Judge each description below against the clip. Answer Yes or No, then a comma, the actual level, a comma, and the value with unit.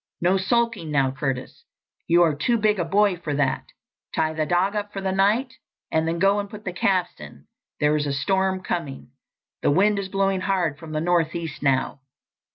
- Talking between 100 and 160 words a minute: No, average, 195 wpm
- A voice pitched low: No, medium, 175 Hz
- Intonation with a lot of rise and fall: No, average, 4.2 semitones